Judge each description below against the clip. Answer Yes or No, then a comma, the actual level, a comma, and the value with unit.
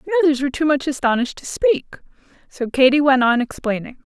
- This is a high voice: Yes, very high, 280 Hz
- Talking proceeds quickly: No, average, 190 wpm